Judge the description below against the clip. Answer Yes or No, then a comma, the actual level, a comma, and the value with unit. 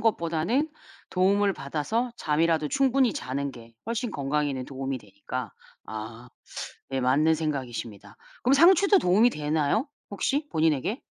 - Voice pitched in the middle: Yes, medium, 155 Hz